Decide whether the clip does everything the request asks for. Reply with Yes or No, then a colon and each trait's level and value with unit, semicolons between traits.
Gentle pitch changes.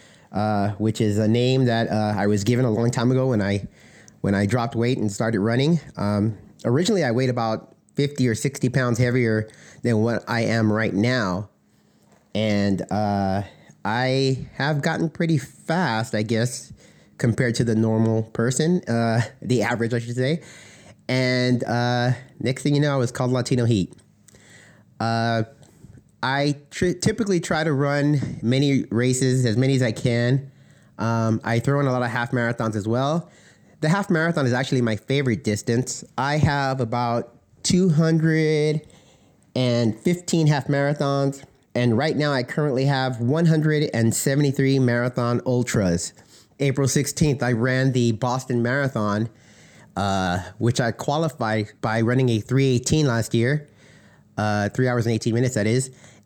No: average, 3.7 semitones